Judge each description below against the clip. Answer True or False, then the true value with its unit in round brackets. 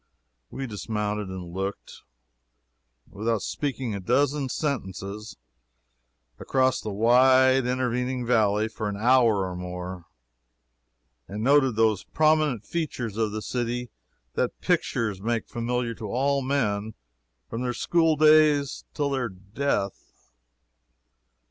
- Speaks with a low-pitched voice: True (120 Hz)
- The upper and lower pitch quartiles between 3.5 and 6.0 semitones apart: True (4.2 semitones)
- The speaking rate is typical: False (115 wpm)